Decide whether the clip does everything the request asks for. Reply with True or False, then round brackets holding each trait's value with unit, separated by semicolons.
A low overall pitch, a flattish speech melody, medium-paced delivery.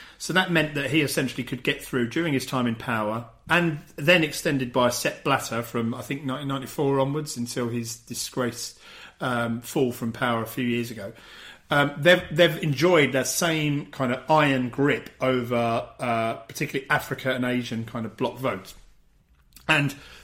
False (130 Hz; 3.7 semitones; 170 wpm)